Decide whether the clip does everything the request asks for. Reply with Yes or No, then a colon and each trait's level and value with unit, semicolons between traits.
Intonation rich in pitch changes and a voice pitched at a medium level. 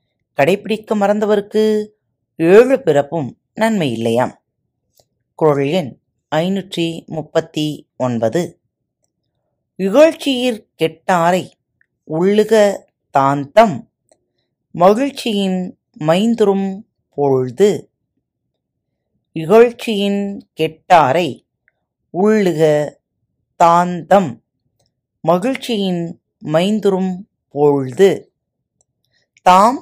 Yes: wide, 6.0 semitones; medium, 180 Hz